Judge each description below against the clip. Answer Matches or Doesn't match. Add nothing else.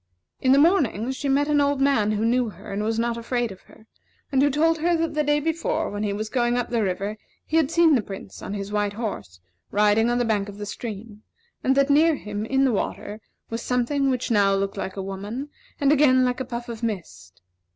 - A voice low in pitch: Doesn't match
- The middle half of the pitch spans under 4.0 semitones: Doesn't match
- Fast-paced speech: Matches